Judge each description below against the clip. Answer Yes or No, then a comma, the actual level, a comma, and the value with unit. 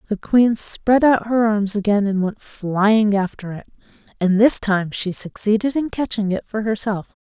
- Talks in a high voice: Yes, high, 210 Hz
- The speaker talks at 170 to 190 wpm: Yes, average, 180 wpm